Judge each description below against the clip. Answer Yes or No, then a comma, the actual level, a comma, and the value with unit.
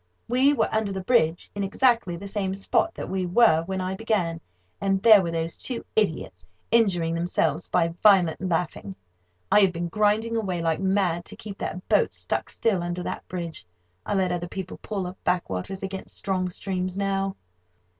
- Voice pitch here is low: No, high, 190 Hz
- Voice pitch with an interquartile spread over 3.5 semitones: No, average, 2.8 semitones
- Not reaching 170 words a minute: No, average, 180 wpm